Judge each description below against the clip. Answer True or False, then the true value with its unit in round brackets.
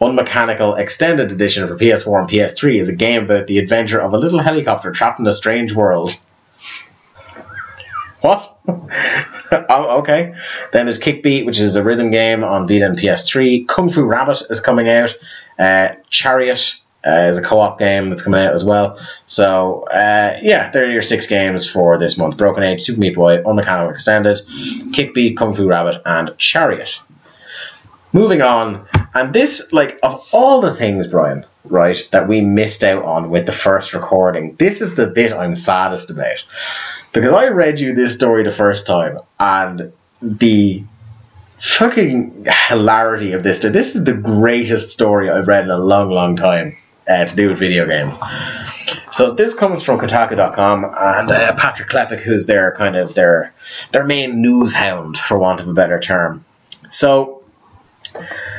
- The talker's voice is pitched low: True (105 Hz)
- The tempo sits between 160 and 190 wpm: True (170 wpm)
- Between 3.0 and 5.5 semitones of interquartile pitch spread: True (3.8 semitones)